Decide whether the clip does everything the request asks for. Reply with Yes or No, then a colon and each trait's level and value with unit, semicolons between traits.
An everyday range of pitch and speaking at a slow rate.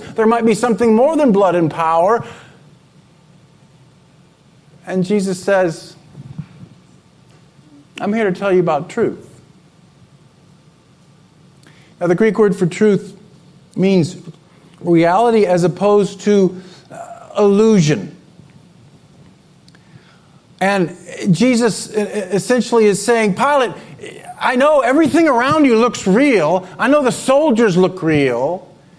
Yes: average, 4.6 semitones; slow, 105 wpm